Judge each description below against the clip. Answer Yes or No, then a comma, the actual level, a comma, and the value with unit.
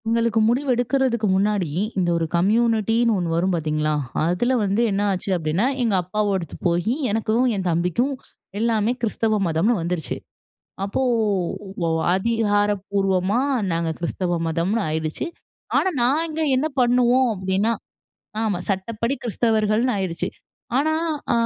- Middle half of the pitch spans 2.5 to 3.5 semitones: No, average, 4.6 semitones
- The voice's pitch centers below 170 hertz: No, high, 205 Hz